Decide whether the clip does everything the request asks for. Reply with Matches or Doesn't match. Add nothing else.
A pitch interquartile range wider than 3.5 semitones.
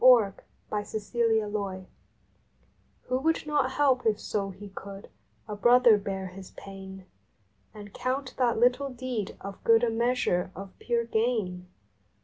Matches